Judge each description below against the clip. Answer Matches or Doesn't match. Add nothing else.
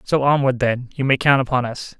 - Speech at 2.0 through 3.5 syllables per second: Doesn't match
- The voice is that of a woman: Doesn't match